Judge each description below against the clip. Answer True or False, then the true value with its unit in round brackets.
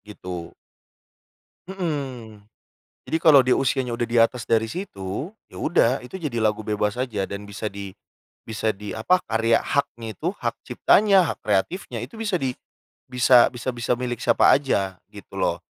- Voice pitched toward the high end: False (120 Hz)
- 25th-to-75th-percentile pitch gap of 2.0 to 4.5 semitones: False (4.9 semitones)